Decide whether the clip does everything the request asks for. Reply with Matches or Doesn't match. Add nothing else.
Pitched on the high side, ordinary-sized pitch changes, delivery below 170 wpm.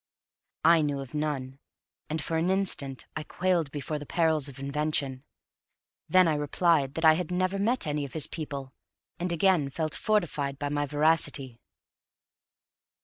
Doesn't match